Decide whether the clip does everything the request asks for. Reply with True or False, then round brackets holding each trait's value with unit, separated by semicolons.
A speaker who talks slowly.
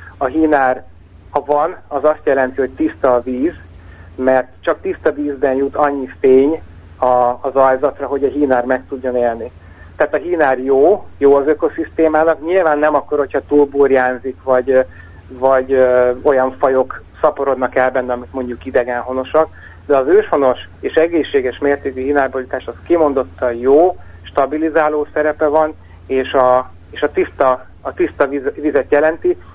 False (150 wpm)